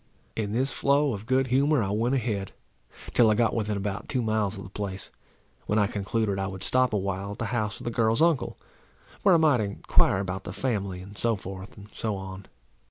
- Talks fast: Yes, fast, 215 wpm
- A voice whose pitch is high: No, low, 105 Hz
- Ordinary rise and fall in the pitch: Yes, average, 3.6 semitones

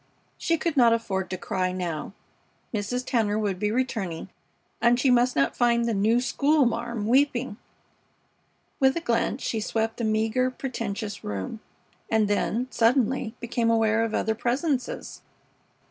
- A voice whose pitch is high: Yes, high, 230 Hz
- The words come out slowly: No, average, 145 wpm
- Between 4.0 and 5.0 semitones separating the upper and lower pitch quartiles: No, average, 3.1 semitones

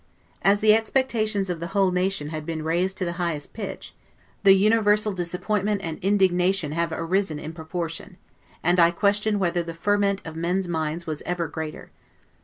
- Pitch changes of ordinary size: Yes, average, 3.3 semitones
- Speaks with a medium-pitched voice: Yes, medium, 180 Hz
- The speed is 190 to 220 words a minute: No, average, 170 wpm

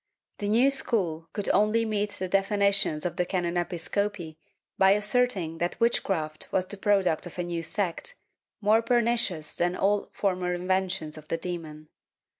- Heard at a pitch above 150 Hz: Yes, high, 190 Hz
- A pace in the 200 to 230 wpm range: No, average, 165 wpm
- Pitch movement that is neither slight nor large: Yes, average, 3.4 semitones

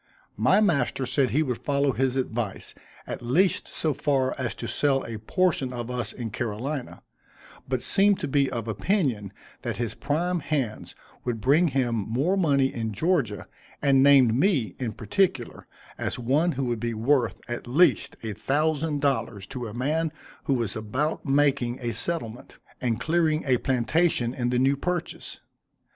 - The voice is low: Yes, low, 130 Hz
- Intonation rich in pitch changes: No, average, 4.2 semitones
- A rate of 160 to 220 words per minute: Yes, average, 165 wpm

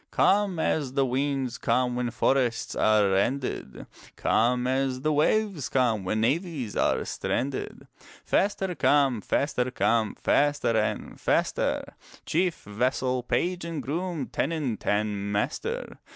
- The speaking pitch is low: Yes, low, 130 Hz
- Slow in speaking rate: Yes, slow, 125 wpm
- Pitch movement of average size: Yes, average, 4.5 semitones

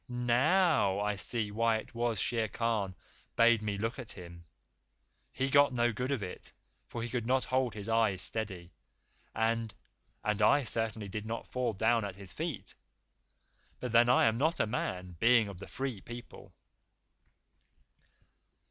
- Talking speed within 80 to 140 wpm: No, average, 160 wpm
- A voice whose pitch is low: Yes, low, 115 Hz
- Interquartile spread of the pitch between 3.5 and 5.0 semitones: No, average, 2.9 semitones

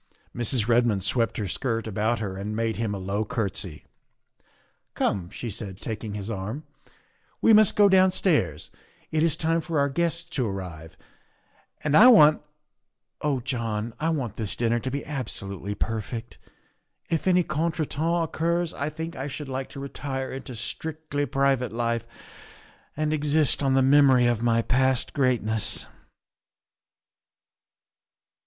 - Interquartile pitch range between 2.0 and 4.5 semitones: No, wide, 5.6 semitones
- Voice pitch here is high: No, low, 130 Hz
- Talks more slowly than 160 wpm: Yes, average, 150 wpm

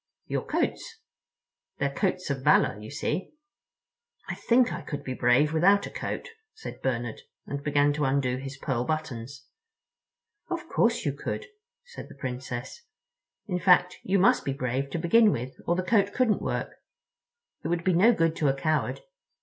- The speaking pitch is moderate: Yes, medium, 150 Hz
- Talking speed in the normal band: Yes, average, 170 wpm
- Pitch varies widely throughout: Yes, wide, 6.6 semitones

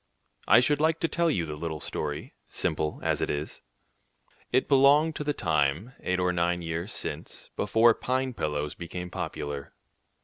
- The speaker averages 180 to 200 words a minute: No, average, 165 wpm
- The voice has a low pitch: Yes, very low, 90 Hz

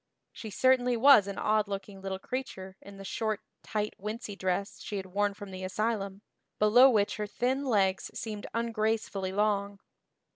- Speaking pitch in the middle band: No, high, 205 Hz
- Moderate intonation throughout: No, narrow, 2.3 semitones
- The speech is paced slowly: No, average, 160 wpm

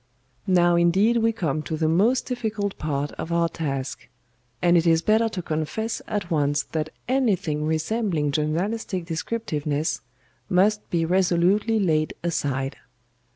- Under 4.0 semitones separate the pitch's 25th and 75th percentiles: No, average, 5.3 semitones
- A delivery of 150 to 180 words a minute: No, slow, 135 wpm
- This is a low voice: No, medium, 170 Hz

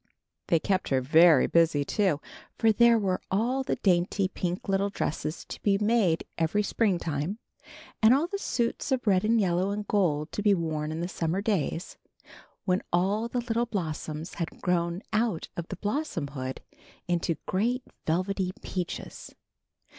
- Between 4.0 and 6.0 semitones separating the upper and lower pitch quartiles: Yes, average, 4.4 semitones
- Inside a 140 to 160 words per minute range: Yes, average, 155 wpm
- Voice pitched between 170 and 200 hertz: Yes, medium, 185 Hz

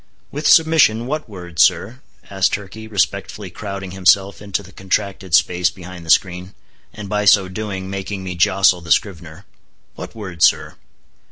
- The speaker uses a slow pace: No, average, 155 wpm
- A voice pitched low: Yes, very low, 95 Hz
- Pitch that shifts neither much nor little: No, narrow, 2.3 semitones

